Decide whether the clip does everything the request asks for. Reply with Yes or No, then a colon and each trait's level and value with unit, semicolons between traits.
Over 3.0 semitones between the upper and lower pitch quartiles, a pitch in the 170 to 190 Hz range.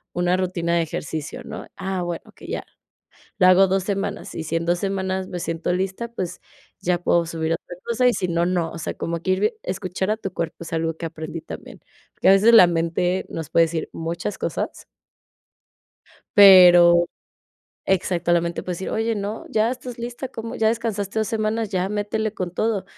Yes: average, 3.4 semitones; medium, 185 Hz